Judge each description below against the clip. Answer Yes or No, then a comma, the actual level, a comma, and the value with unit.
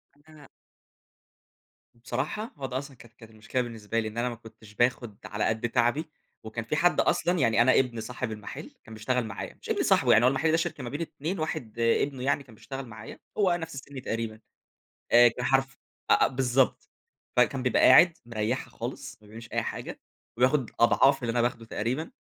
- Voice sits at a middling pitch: No, low, 125 Hz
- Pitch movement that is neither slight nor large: Yes, average, 3.2 semitones